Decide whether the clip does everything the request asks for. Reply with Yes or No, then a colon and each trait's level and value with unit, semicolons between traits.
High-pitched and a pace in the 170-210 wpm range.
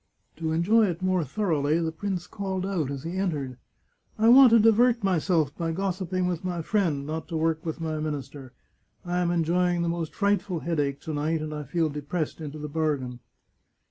No: medium, 165 Hz; average, 200 wpm